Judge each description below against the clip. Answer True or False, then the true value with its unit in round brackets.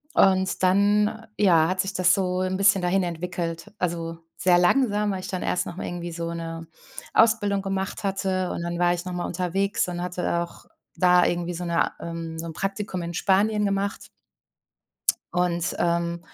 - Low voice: False (180 Hz)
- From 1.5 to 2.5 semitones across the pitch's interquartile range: True (2.2 semitones)